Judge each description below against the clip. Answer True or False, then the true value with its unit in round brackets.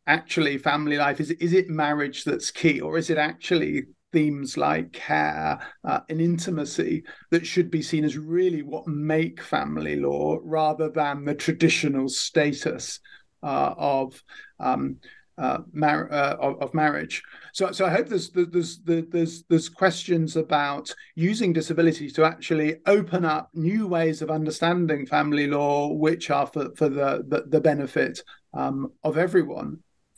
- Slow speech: False (155 wpm)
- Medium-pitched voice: True (155 Hz)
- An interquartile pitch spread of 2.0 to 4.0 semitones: True (2.5 semitones)